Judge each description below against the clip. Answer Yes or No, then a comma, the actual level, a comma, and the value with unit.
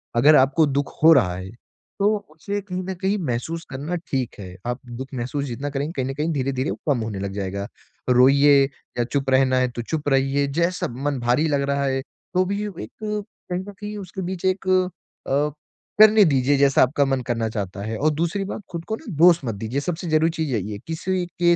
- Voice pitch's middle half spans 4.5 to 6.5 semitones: Yes, average, 5.2 semitones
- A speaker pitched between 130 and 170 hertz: Yes, medium, 140 Hz